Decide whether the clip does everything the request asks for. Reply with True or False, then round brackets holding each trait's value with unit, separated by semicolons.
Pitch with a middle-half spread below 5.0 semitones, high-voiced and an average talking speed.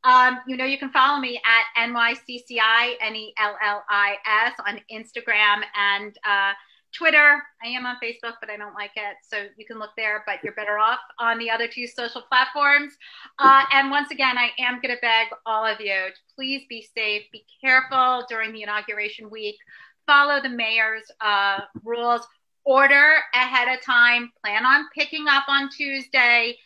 True (3.6 semitones; 235 Hz; 170 wpm)